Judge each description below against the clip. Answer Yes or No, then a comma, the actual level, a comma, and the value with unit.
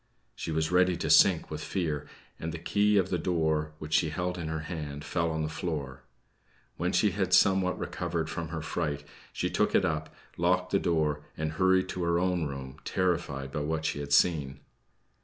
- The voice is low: Yes, very low, 80 Hz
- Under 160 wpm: No, average, 195 wpm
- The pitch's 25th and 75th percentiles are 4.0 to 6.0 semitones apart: No, average, 2.8 semitones